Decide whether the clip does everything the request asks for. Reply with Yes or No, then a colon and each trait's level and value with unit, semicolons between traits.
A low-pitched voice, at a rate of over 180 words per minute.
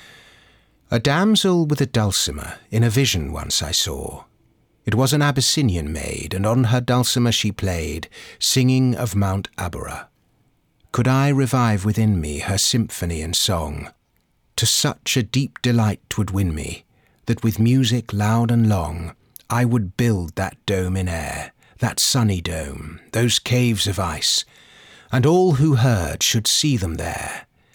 No: low, 110 Hz; average, 155 wpm